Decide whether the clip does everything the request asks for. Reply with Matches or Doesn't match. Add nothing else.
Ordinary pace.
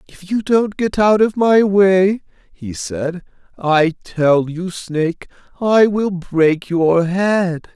Matches